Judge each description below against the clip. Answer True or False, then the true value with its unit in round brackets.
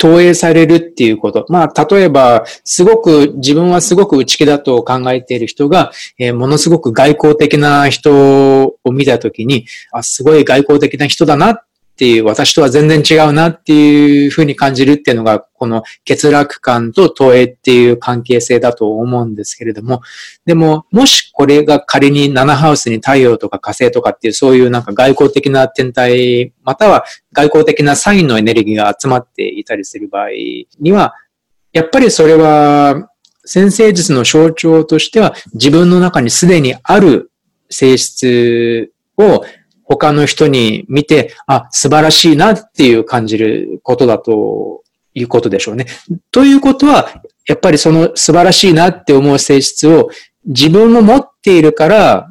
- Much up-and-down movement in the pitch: False (4.9 semitones)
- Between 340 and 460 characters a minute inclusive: False (325 characters per minute)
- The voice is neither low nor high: True (145 Hz)